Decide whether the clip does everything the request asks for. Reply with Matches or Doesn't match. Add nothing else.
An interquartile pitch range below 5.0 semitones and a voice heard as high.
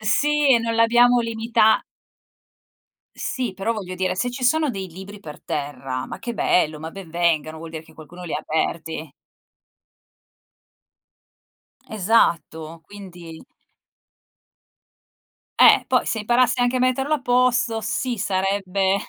Doesn't match